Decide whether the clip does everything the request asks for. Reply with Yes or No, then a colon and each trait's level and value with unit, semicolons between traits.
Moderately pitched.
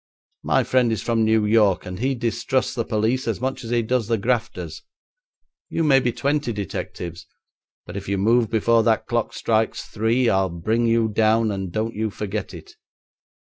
No: low, 115 Hz